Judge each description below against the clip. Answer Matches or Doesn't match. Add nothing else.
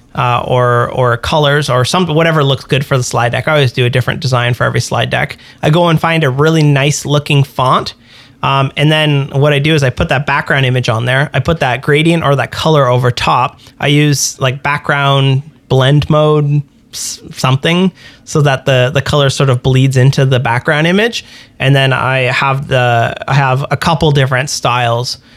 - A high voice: Doesn't match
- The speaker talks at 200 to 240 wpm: Matches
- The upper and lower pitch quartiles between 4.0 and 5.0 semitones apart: Doesn't match